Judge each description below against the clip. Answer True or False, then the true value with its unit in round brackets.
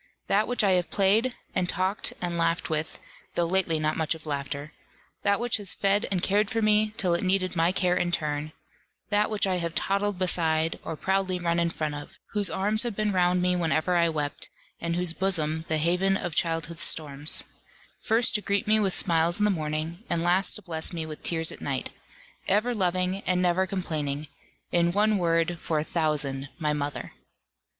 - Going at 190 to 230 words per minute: True (195 wpm)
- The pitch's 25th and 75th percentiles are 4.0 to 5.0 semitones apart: False (3.4 semitones)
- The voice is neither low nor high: True (175 Hz)